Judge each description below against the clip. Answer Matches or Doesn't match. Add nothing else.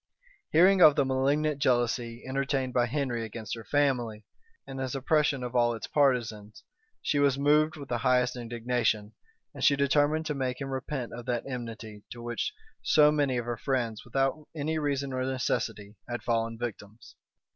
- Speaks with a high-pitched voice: Doesn't match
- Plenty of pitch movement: Doesn't match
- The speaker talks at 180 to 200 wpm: Doesn't match